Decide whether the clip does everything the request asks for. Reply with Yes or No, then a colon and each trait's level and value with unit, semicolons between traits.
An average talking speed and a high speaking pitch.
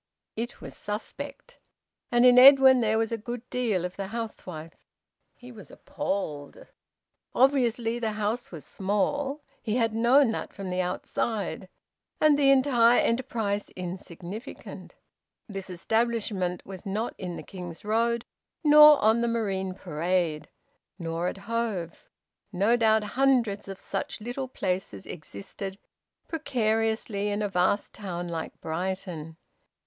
No: slow, 130 wpm; high, 215 Hz